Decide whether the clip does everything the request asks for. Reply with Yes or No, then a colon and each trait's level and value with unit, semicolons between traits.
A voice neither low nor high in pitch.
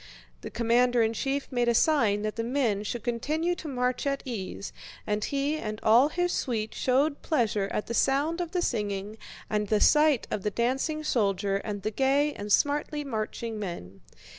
No: high, 240 Hz